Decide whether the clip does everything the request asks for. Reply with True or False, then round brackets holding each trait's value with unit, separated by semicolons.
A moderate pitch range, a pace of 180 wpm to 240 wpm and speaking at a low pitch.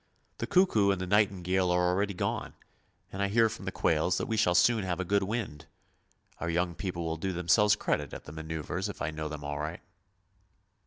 True (3.7 semitones; 205 wpm; 90 Hz)